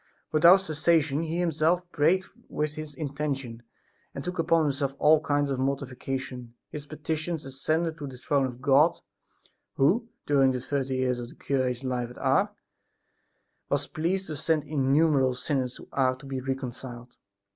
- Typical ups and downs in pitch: Yes, average, 3.1 semitones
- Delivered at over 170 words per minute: No, average, 155 wpm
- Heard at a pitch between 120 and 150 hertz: Yes, medium, 140 Hz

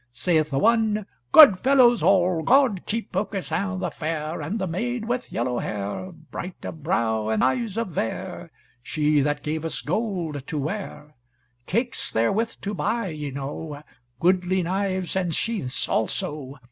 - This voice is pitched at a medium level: Yes, medium, 175 Hz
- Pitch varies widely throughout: Yes, wide, 5.9 semitones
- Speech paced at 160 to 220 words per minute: No, average, 150 wpm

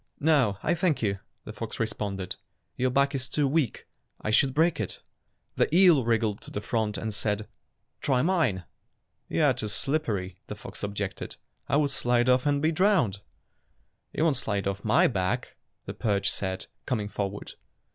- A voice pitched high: No, low, 115 Hz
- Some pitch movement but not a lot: No, wide, 5.8 semitones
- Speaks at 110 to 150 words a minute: No, average, 170 wpm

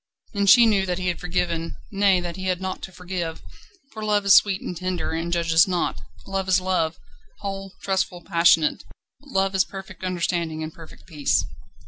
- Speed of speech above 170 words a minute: Yes, average, 180 wpm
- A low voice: No, medium, 185 Hz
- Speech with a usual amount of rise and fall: No, narrow, 2.3 semitones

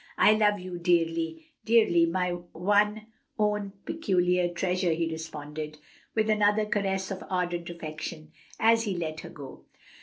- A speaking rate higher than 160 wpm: No, average, 140 wpm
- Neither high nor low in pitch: Yes, medium, 180 Hz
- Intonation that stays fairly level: No, average, 4.0 semitones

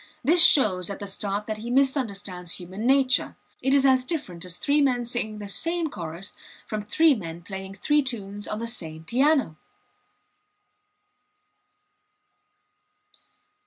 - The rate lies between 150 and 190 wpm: No, slow, 135 wpm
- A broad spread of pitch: Yes, wide, 5.8 semitones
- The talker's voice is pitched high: Yes, high, 215 Hz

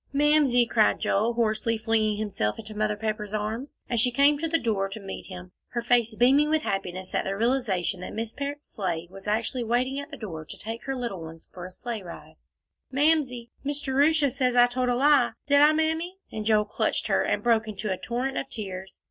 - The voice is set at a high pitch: Yes, high, 230 Hz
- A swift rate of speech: Yes, fast, 215 wpm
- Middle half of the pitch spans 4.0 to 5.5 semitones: Yes, average, 4.4 semitones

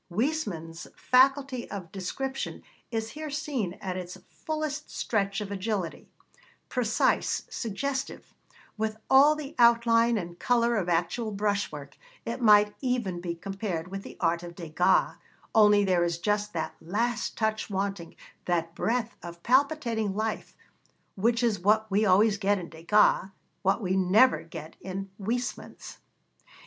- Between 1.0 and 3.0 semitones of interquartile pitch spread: No, average, 4.5 semitones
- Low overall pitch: No, high, 210 Hz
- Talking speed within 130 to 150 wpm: Yes, average, 140 wpm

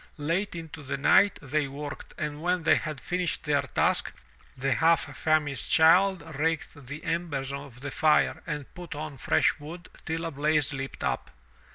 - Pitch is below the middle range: No, medium, 155 Hz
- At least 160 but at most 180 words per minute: Yes, average, 170 wpm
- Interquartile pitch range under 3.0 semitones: Yes, narrow, 2.6 semitones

